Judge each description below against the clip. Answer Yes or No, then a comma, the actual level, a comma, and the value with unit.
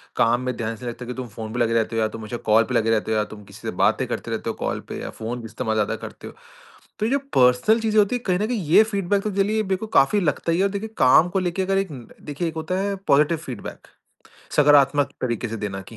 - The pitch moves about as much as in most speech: No, wide, 9.0 semitones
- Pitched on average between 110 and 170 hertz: Yes, medium, 140 Hz